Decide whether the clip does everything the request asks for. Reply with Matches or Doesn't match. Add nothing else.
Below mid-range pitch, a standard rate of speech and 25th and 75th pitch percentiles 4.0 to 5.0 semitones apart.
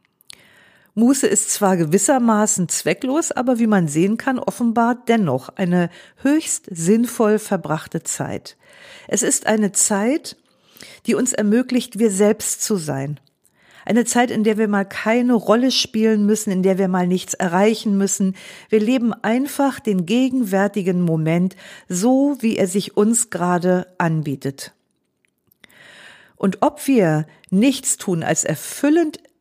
Doesn't match